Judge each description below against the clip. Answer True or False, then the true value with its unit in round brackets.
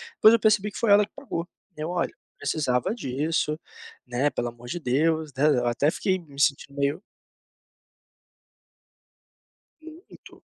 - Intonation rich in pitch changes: True (6.4 semitones)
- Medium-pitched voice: True (155 Hz)